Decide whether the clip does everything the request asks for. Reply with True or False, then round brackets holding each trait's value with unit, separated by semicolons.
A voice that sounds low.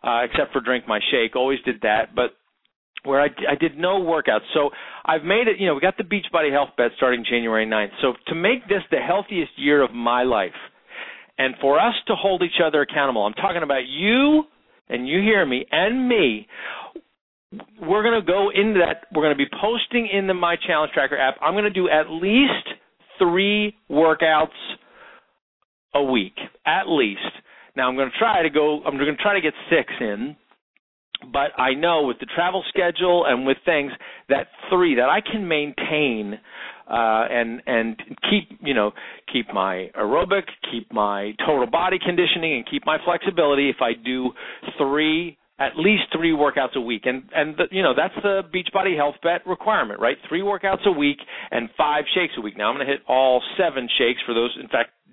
False (155 Hz)